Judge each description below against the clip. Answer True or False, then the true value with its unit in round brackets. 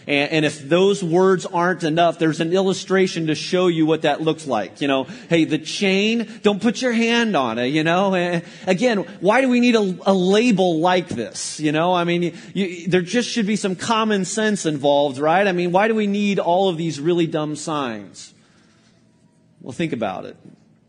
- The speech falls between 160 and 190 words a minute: False (200 wpm)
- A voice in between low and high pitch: True (180 Hz)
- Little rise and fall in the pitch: False (4.0 semitones)